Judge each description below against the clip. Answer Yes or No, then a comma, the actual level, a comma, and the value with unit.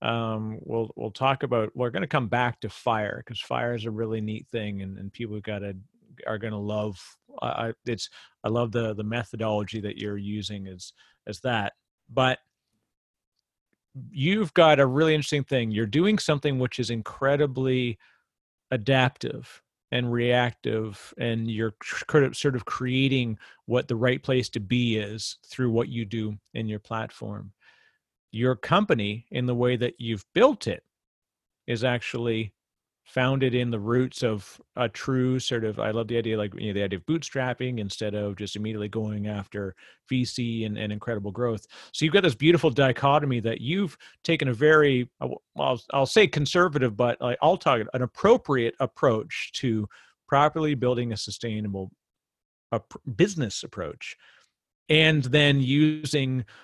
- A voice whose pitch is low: Yes, low, 120 Hz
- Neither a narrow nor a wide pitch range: Yes, average, 3.4 semitones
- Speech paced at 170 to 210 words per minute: No, average, 160 wpm